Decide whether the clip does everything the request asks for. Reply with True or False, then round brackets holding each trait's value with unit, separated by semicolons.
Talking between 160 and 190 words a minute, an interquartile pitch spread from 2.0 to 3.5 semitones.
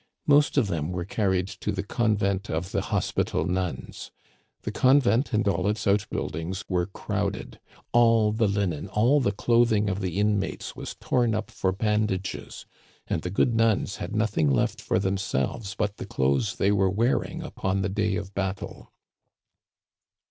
True (165 wpm; 2.5 semitones)